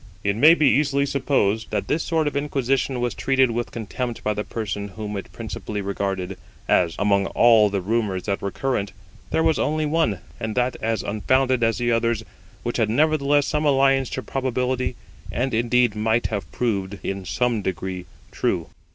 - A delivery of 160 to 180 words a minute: Yes, average, 175 wpm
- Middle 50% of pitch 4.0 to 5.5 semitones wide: Yes, average, 4.6 semitones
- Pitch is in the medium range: No, low, 115 Hz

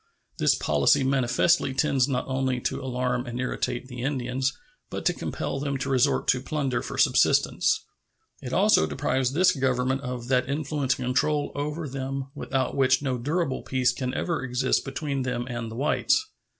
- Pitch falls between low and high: No, low, 130 Hz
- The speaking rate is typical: Yes, average, 170 wpm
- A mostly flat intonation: Yes, narrow, 1.8 semitones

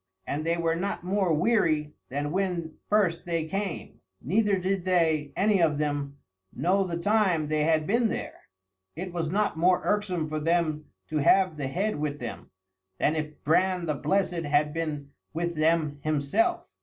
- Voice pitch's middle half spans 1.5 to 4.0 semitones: Yes, average, 3.7 semitones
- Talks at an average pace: Yes, average, 170 wpm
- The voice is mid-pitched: Yes, medium, 165 Hz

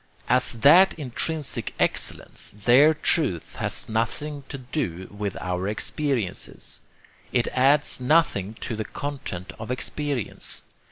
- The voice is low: Yes, low, 125 Hz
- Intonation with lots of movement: Yes, wide, 6.0 semitones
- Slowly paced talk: Yes, slow, 115 wpm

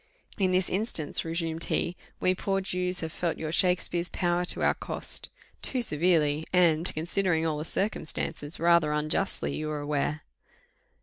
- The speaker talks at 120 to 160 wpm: Yes, average, 150 wpm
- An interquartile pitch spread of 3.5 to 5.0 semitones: No, average, 2.8 semitones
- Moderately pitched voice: Yes, medium, 170 Hz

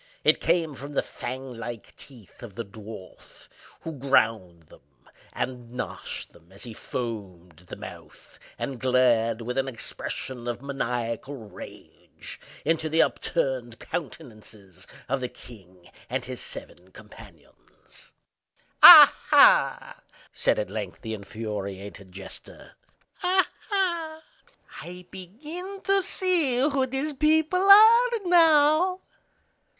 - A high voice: No, low, 125 Hz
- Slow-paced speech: Yes, slow, 120 wpm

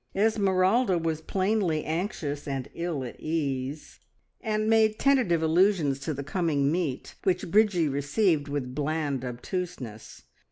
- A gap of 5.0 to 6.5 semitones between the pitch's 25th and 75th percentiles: Yes, average, 5.3 semitones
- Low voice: No, medium, 160 Hz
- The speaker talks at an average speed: No, slow, 125 wpm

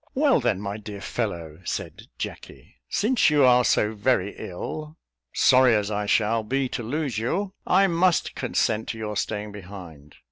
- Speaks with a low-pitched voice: Yes, low, 110 Hz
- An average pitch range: No, wide, 5.9 semitones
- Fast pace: No, average, 165 wpm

